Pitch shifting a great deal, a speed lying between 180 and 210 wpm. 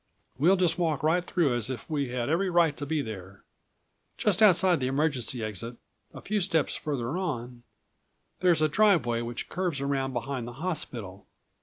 No: wide, 6.2 semitones; average, 170 wpm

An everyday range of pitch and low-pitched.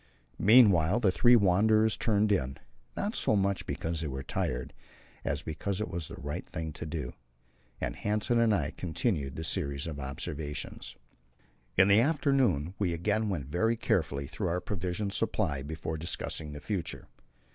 No: wide, 6.2 semitones; very low, 90 Hz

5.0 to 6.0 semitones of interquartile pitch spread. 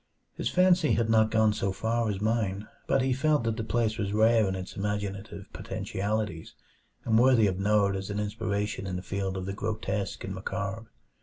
No: narrow, 2.4 semitones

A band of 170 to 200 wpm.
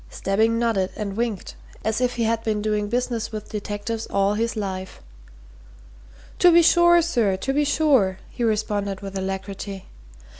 No: average, 155 wpm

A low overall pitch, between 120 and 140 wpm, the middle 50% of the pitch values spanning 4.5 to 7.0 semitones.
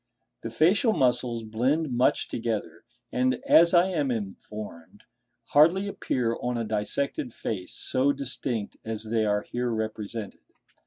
No: low, 120 Hz; slow, 135 wpm; average, 4.1 semitones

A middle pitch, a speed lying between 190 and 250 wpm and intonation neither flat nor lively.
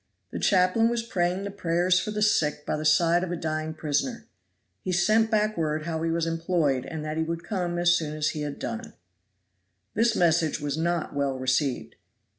Yes: medium, 170 Hz; average, 200 wpm; average, 3.2 semitones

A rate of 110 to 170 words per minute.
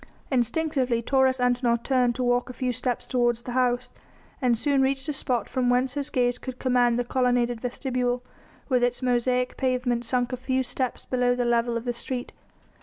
No: average, 185 wpm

